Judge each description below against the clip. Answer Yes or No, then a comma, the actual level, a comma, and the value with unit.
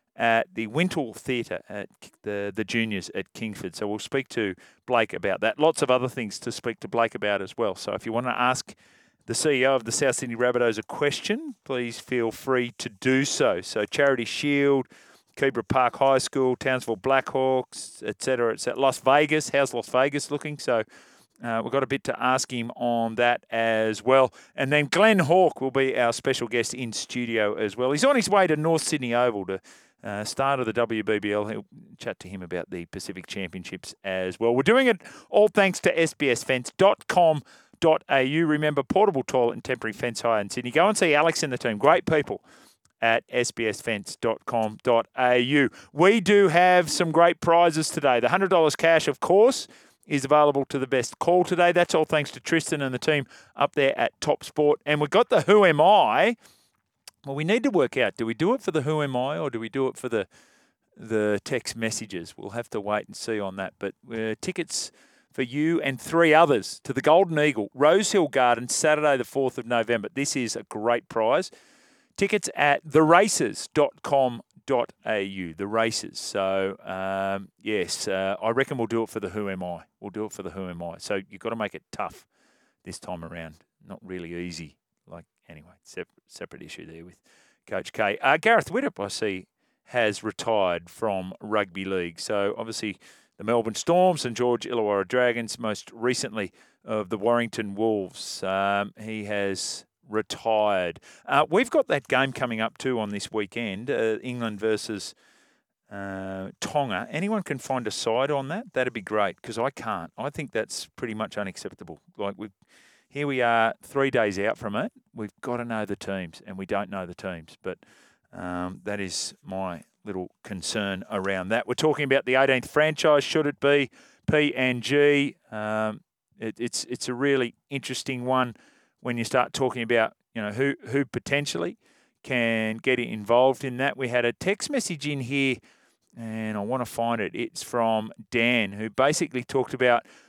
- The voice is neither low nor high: No, low, 125 Hz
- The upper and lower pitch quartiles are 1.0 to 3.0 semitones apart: No, average, 4.7 semitones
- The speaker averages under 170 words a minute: No, average, 190 wpm